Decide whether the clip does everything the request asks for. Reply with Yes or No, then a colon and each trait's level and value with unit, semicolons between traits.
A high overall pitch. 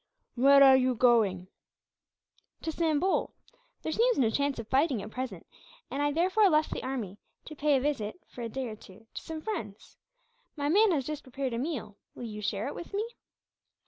Yes: very high, 270 Hz